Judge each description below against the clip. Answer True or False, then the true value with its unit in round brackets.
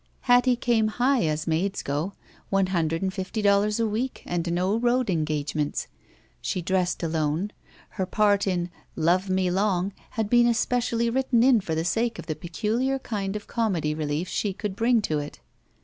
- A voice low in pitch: False (195 Hz)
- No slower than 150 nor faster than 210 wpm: True (175 wpm)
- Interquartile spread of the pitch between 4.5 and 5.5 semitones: True (5.1 semitones)